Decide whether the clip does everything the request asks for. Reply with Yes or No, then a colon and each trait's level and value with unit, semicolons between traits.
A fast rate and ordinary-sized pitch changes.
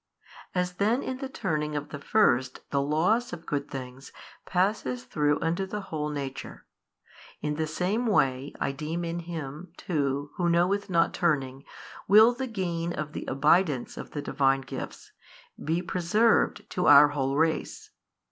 No: average, 155 wpm; average, 4.5 semitones